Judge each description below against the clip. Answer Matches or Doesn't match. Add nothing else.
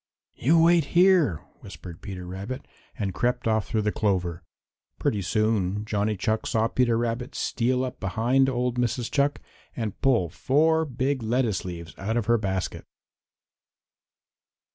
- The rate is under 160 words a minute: Matches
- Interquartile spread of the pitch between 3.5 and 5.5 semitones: Matches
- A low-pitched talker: Matches